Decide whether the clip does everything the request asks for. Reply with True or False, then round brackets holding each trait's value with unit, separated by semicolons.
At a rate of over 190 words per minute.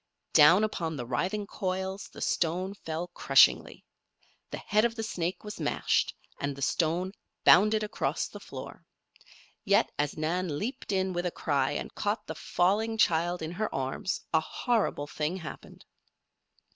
False (155 wpm)